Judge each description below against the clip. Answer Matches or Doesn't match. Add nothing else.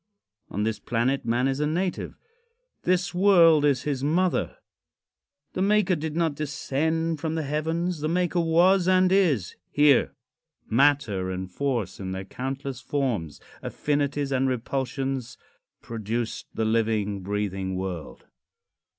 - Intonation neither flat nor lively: Doesn't match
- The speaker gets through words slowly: Matches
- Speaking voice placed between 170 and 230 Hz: Doesn't match